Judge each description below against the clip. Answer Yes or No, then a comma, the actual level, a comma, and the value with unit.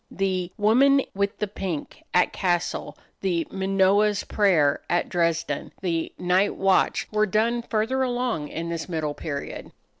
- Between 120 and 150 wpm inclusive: Yes, average, 140 wpm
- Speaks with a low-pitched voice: No, high, 190 Hz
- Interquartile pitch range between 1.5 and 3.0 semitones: No, average, 3.9 semitones